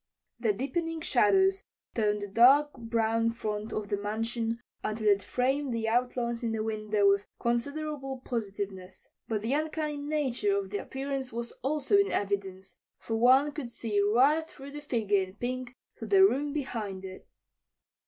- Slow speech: No, average, 160 wpm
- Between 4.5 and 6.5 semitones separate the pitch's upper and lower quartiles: Yes, average, 5.1 semitones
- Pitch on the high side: Yes, high, 235 Hz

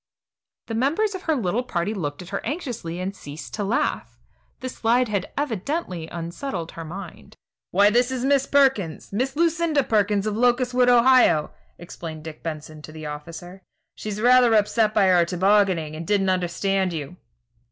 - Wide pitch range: Yes, wide, 6.5 semitones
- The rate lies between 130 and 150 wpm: No, average, 165 wpm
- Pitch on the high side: Yes, high, 205 Hz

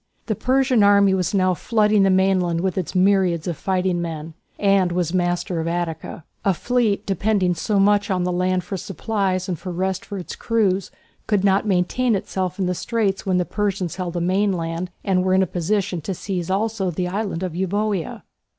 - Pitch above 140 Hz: Yes, high, 190 Hz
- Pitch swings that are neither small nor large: No, narrow, 2.2 semitones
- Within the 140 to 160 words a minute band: No, average, 195 wpm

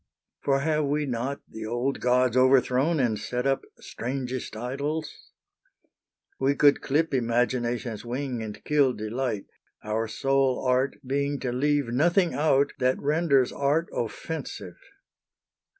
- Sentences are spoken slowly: Yes, slow, 125 wpm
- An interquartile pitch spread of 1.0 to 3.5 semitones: Yes, average, 2.7 semitones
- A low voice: Yes, low, 130 Hz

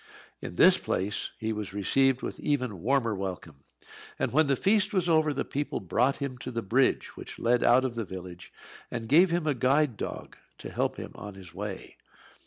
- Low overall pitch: Yes, low, 125 Hz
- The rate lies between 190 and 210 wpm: Yes, average, 195 wpm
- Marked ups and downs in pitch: Yes, wide, 5.7 semitones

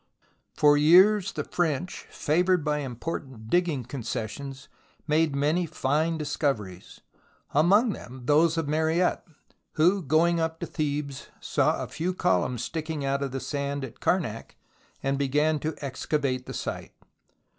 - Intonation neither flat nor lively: Yes, average, 3.2 semitones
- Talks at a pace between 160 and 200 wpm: No, slow, 135 wpm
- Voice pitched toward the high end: No, medium, 150 Hz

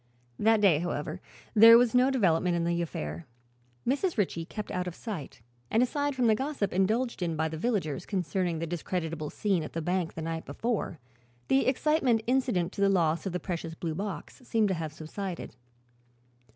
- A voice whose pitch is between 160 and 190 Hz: Yes, medium, 185 Hz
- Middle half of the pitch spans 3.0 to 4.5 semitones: No, wide, 5.6 semitones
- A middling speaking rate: Yes, average, 185 wpm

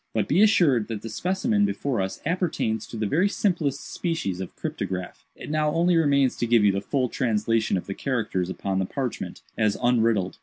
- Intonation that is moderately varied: No, wide, 7.7 semitones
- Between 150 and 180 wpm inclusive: No, average, 195 wpm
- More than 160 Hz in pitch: No, low, 120 Hz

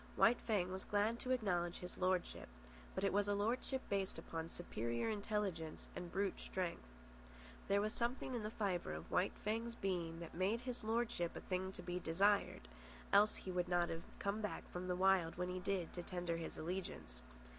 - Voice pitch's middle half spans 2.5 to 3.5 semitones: Yes, average, 3.1 semitones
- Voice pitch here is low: No, high, 190 Hz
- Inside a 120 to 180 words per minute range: No, average, 190 wpm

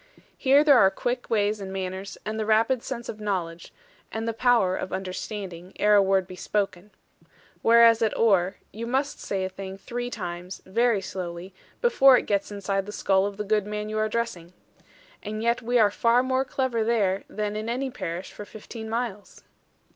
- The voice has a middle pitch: No, high, 210 Hz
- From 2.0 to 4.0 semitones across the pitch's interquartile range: Yes, average, 3.4 semitones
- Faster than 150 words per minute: Yes, average, 190 wpm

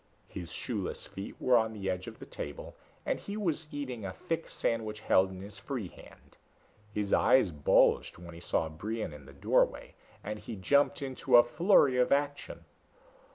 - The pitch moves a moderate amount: No, wide, 6.6 semitones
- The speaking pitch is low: Yes, low, 110 Hz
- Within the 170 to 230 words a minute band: Yes, average, 180 wpm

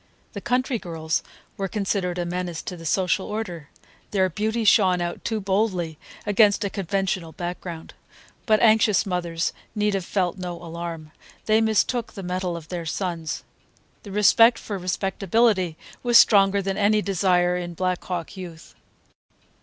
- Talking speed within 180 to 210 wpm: No, average, 150 wpm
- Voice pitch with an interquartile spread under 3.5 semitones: Yes, average, 3.1 semitones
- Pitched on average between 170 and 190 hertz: Yes, medium, 185 Hz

